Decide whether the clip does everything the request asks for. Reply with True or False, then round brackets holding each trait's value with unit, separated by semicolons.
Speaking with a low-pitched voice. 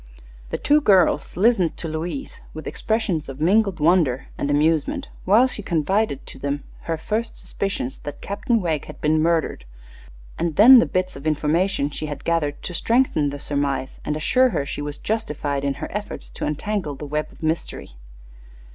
False (160 Hz)